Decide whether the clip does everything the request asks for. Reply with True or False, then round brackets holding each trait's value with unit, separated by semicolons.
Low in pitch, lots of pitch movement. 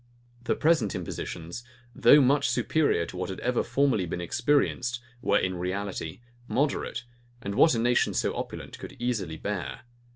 True (115 Hz; 6.3 semitones)